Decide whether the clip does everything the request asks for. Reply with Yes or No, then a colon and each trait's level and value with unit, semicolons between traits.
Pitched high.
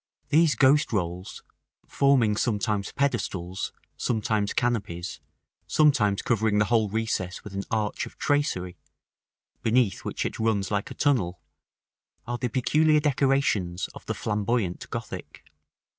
No: low, 110 Hz